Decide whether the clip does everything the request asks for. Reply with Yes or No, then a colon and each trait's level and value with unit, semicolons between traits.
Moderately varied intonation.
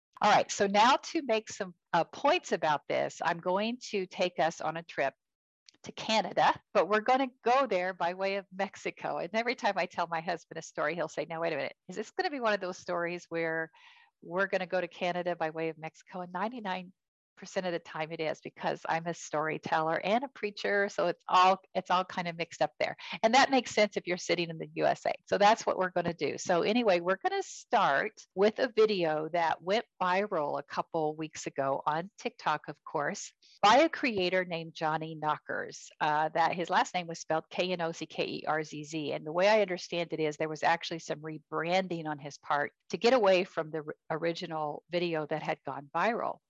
Yes: average, 3.9 semitones